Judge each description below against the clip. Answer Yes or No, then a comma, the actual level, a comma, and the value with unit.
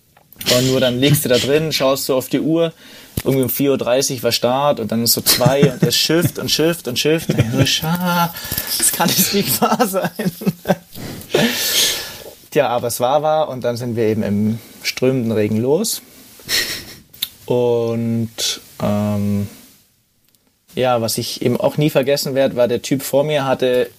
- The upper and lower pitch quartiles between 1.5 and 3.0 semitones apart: No, average, 4.8 semitones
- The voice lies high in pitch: No, low, 135 Hz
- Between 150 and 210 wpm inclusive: Yes, average, 175 wpm